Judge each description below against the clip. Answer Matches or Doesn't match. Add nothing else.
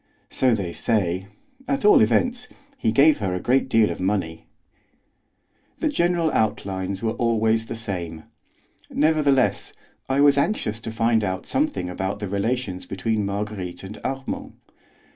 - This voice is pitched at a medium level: Doesn't match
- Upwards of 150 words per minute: Doesn't match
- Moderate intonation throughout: Doesn't match